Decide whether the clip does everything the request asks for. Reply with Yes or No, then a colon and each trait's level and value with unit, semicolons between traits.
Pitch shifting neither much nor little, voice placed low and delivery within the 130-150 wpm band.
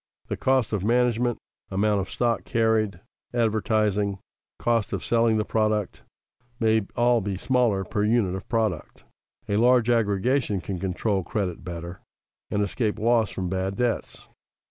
Yes: average, 3.1 semitones; low, 110 Hz; average, 145 wpm